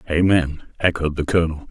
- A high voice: No, very low, 80 Hz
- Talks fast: No, average, 140 wpm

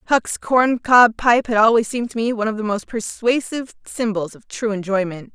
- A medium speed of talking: Yes, average, 190 wpm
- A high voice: Yes, high, 225 Hz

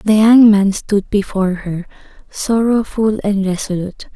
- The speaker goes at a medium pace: No, slow, 130 wpm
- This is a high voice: Yes, high, 205 Hz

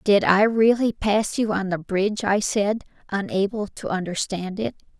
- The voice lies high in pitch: Yes, high, 200 Hz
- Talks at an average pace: Yes, average, 170 wpm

